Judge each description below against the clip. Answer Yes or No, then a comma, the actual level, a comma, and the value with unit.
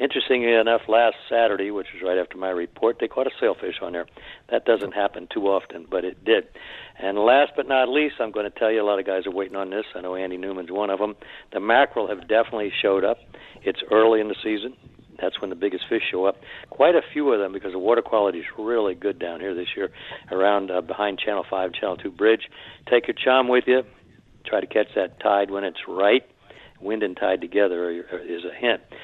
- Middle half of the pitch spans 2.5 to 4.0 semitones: Yes, average, 3.4 semitones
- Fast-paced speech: Yes, fast, 230 wpm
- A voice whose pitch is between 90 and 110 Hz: Yes, low, 105 Hz